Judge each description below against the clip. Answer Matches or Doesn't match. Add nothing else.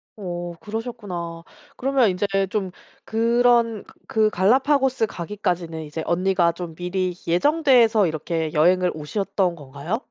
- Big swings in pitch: Doesn't match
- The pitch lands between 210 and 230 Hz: Doesn't match